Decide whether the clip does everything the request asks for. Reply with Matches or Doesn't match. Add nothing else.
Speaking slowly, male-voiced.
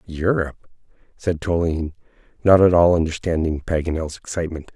Matches